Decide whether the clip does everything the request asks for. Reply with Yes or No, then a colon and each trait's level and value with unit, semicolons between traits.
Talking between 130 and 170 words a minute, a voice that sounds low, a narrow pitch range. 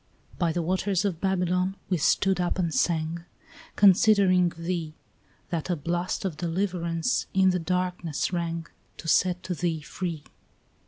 No: average, 140 wpm; medium, 175 Hz; narrow, 1.9 semitones